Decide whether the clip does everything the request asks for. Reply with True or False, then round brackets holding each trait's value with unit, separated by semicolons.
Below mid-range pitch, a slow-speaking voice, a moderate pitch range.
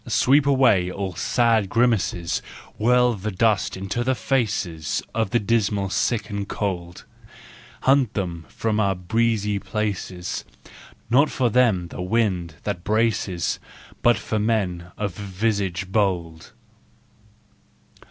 True (105 Hz; 120 wpm; 3.9 semitones)